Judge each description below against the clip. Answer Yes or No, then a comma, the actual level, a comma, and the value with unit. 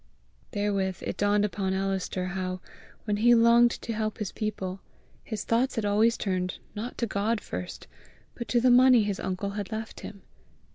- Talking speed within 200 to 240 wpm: No, average, 175 wpm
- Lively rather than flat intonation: No, average, 3.1 semitones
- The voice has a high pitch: Yes, high, 210 Hz